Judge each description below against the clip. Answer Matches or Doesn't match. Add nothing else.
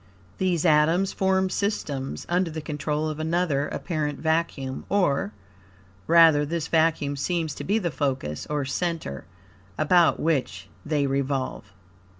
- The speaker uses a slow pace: Matches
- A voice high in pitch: Doesn't match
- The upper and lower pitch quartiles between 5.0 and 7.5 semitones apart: Doesn't match